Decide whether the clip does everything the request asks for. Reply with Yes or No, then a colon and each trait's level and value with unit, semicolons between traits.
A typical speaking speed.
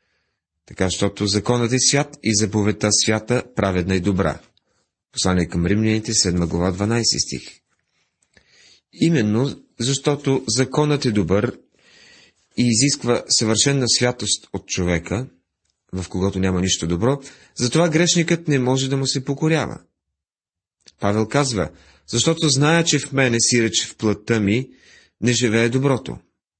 Yes: average, 130 wpm